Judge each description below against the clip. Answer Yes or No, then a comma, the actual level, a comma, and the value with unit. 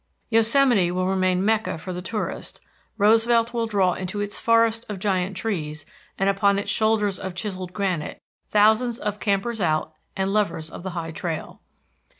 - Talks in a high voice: Yes, high, 200 Hz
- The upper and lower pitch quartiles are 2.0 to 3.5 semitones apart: Yes, average, 3.2 semitones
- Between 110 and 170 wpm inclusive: Yes, average, 160 wpm